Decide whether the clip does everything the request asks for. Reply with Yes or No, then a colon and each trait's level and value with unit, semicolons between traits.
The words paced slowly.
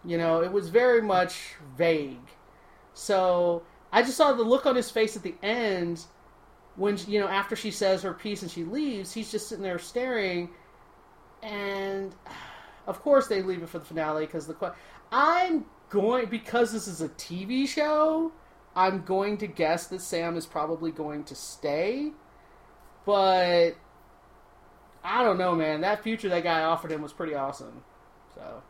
No: average, 165 wpm